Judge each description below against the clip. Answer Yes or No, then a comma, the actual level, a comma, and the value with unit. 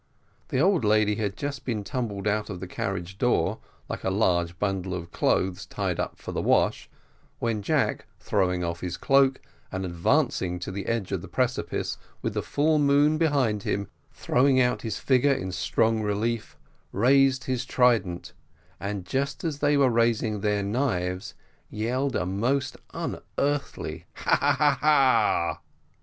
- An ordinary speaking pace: Yes, average, 160 wpm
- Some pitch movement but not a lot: No, wide, 5.9 semitones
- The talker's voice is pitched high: No, low, 110 Hz